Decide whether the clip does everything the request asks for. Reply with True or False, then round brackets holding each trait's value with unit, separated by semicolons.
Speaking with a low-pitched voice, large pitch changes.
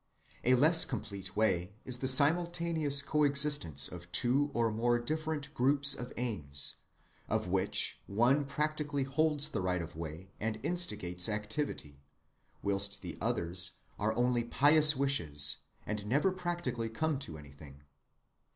True (120 Hz; 7.4 semitones)